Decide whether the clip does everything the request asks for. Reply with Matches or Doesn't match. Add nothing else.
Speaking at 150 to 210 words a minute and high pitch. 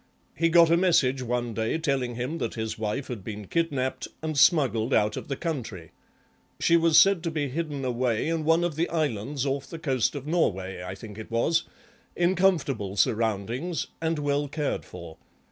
Doesn't match